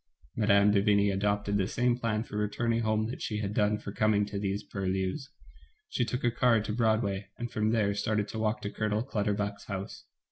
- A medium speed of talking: No, fast, 210 wpm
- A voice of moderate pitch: No, low, 105 Hz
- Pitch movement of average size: No, narrow, 1.7 semitones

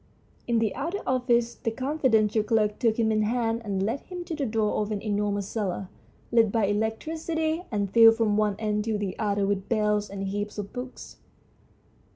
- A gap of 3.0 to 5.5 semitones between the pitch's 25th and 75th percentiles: No, narrow, 2.5 semitones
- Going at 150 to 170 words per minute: No, average, 190 wpm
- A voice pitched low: No, high, 220 Hz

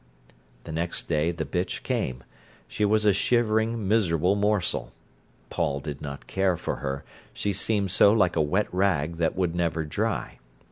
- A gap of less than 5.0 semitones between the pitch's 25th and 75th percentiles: Yes, average, 4.3 semitones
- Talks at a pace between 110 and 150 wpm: No, average, 160 wpm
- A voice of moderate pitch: No, very low, 90 Hz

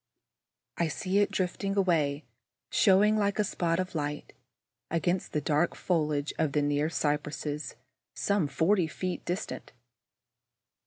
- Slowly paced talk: Yes, slow, 125 wpm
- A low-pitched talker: No, medium, 165 Hz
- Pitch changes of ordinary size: Yes, average, 4.2 semitones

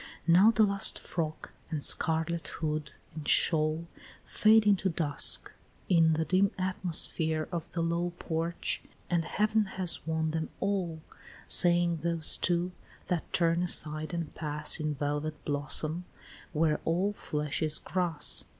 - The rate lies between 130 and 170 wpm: Yes, slow, 135 wpm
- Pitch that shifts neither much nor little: No, narrow, 2.3 semitones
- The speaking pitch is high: No, medium, 165 Hz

